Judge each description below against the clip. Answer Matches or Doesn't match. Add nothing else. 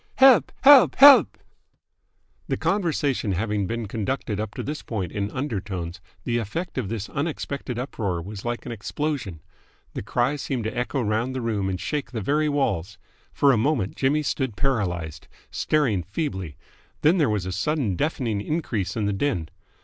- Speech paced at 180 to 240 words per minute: Doesn't match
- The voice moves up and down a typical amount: Doesn't match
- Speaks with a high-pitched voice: Doesn't match